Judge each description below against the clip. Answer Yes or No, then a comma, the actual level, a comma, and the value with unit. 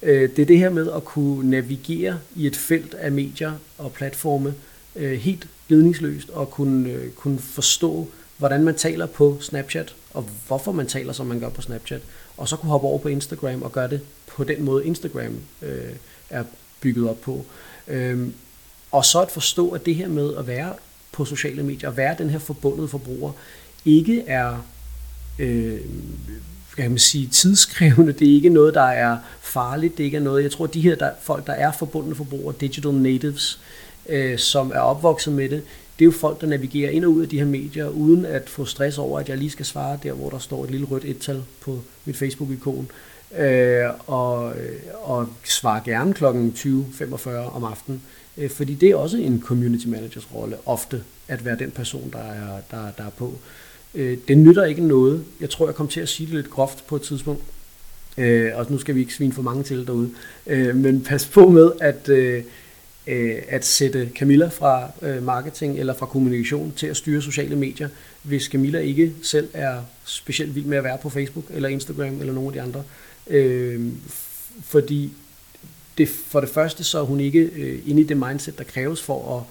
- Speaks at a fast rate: No, average, 190 wpm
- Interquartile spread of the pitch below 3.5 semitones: Yes, average, 2.7 semitones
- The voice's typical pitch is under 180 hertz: Yes, medium, 140 Hz